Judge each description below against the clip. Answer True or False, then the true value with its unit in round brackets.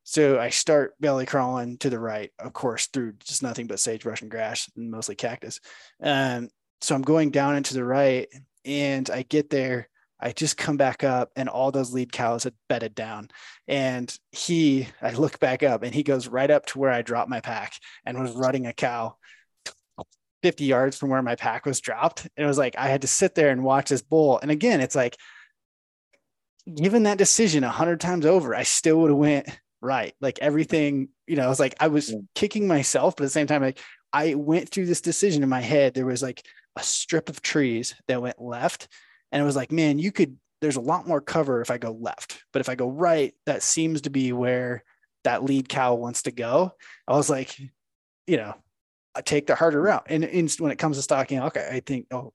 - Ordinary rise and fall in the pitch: True (3.4 semitones)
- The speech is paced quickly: True (220 wpm)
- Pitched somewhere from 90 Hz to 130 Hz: False (140 Hz)